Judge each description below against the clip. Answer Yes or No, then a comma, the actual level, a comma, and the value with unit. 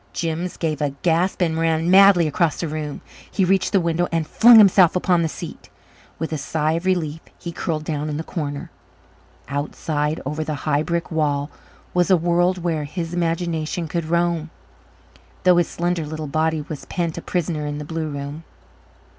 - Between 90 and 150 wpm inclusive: No, average, 180 wpm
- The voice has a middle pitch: Yes, medium, 165 Hz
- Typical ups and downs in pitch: No, narrow, 2.3 semitones